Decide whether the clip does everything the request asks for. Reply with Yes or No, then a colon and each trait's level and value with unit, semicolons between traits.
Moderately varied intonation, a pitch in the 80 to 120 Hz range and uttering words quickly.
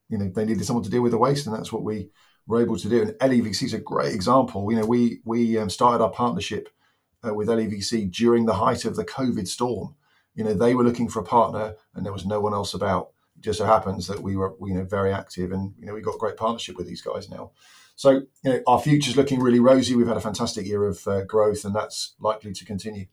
Yes: average, 3.0 semitones; low, 110 Hz; fast, 265 wpm